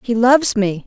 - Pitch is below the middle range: No, high, 230 Hz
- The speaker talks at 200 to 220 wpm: Yes, fast, 210 wpm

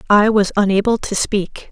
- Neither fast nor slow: Yes, average, 175 wpm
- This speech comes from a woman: Yes, female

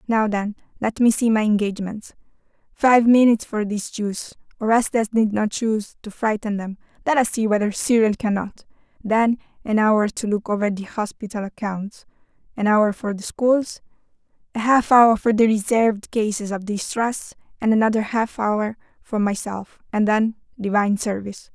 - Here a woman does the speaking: Yes, female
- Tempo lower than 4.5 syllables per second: No, 5.0 syllables/s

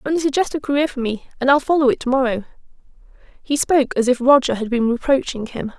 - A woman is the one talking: Yes, female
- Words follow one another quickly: Yes, fast, 220 wpm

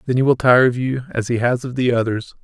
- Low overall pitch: Yes, low, 125 Hz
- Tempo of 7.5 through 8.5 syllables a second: No, 6.0 syllables/s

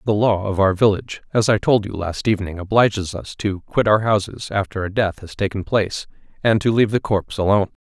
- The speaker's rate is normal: No, fast, 230 wpm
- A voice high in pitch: No, low, 100 Hz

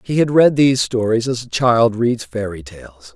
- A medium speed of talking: No, fast, 210 wpm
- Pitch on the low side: Yes, low, 115 Hz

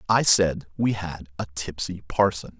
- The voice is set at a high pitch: No, very low, 90 Hz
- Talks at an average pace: Yes, average, 160 wpm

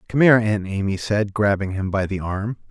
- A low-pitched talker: Yes, low, 100 Hz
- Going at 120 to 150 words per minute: No, average, 200 wpm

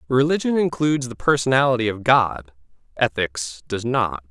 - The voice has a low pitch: Yes, low, 120 Hz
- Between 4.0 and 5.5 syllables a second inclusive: Yes, 5.0 syllables/s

